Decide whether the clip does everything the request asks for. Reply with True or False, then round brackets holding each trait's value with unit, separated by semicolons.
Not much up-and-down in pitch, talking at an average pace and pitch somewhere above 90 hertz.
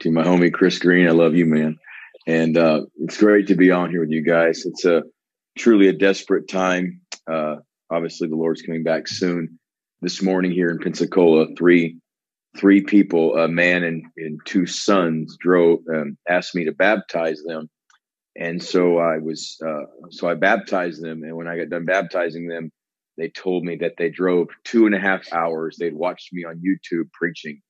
False (1.7 semitones; 190 wpm; 85 Hz)